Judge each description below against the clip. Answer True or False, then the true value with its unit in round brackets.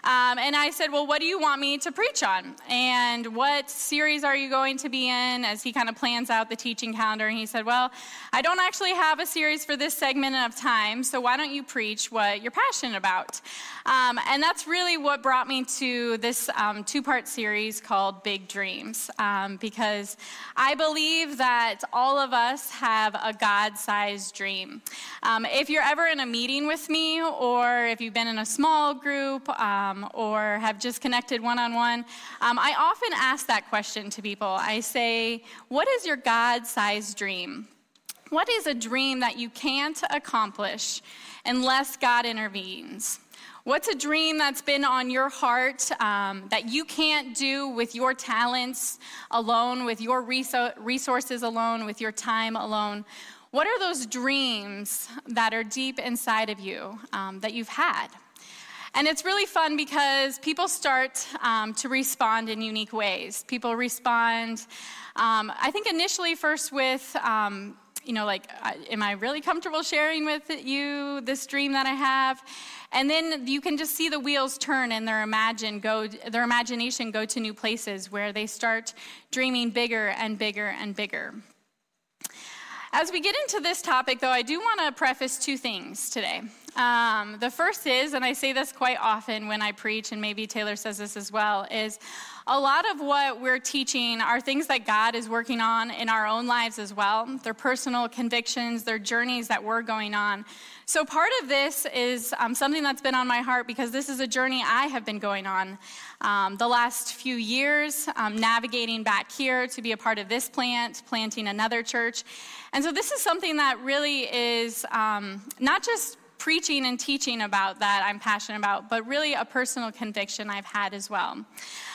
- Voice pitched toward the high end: True (245 Hz)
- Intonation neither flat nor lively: True (4.0 semitones)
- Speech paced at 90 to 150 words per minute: False (185 wpm)